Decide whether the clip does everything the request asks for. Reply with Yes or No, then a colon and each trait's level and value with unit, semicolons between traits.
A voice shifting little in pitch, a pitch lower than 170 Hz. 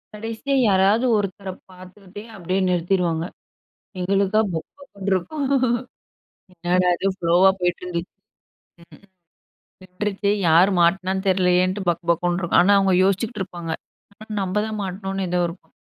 No: narrow, 2.0 semitones; high, 190 Hz